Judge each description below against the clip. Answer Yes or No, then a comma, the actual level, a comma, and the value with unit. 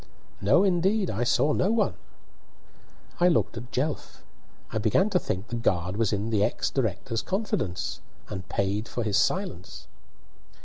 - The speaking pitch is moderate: No, low, 115 Hz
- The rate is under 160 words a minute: Yes, average, 150 wpm